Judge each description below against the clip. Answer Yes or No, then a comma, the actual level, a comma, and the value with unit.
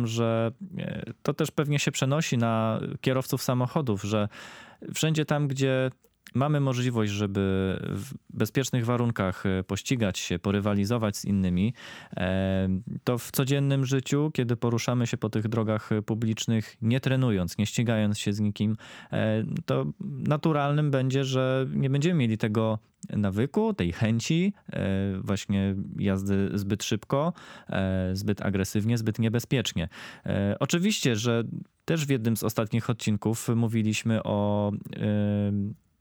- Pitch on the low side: Yes, low, 115 Hz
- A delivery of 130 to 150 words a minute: No, average, 120 wpm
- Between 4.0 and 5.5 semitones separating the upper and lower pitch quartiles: Yes, average, 4.5 semitones